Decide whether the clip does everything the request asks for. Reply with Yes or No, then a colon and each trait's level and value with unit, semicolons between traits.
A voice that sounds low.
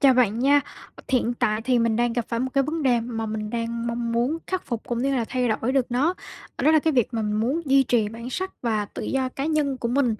No: high, 245 Hz